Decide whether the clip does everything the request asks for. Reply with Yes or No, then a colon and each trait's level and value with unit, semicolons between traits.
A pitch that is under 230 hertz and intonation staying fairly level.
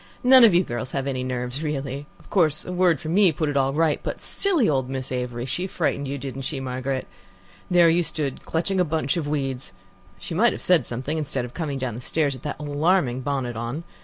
No: medium, 140 Hz; average, 3.9 semitones